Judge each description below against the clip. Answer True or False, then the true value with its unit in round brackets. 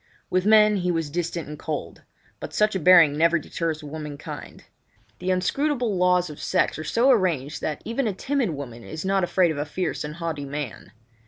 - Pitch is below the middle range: False (170 Hz)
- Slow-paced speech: False (190 wpm)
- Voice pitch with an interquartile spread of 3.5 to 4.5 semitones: True (4.1 semitones)